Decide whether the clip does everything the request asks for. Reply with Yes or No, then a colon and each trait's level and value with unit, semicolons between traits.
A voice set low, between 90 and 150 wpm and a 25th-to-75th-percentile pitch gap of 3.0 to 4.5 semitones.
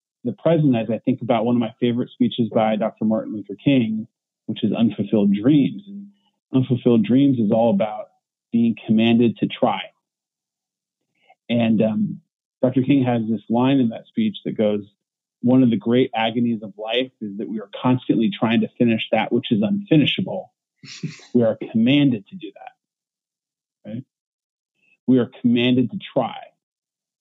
No: low, 120 Hz; average, 160 wpm; average, 4.0 semitones